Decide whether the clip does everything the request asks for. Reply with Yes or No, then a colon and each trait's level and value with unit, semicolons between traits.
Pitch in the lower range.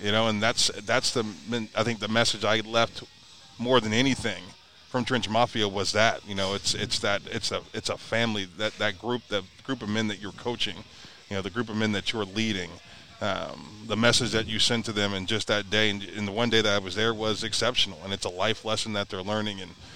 Yes: low, 110 Hz